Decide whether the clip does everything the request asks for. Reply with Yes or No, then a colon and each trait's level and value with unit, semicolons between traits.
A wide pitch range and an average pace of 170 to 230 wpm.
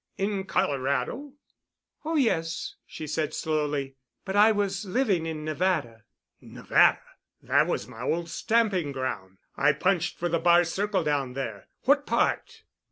No: wide, 6.0 semitones; average, 140 wpm